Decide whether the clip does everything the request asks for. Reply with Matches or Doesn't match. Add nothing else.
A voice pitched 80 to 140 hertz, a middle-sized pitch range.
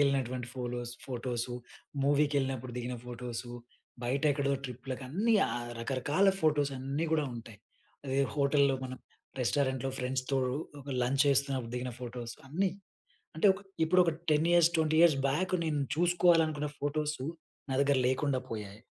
Matches